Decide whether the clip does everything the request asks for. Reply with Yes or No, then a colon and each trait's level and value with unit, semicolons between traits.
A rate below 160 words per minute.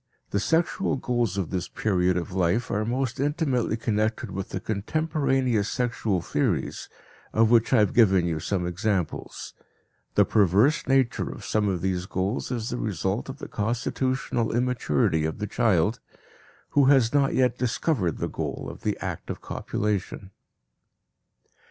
Yes: average, 150 wpm